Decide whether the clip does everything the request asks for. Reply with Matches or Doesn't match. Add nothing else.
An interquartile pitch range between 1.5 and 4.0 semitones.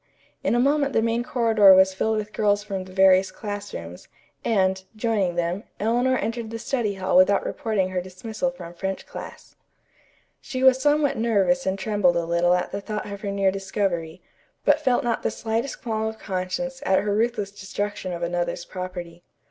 Matches